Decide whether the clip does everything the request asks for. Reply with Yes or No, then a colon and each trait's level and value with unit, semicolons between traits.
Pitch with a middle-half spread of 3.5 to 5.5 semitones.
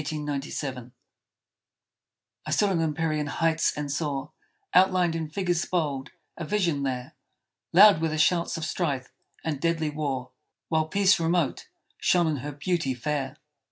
No: average, 3.1 semitones